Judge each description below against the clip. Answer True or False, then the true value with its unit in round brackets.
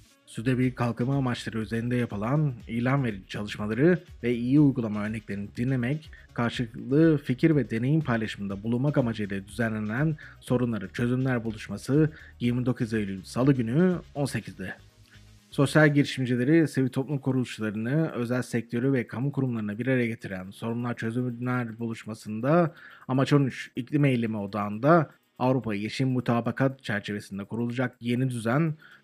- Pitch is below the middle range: True (120 Hz)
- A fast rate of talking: False (120 wpm)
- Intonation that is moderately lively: True (3.5 semitones)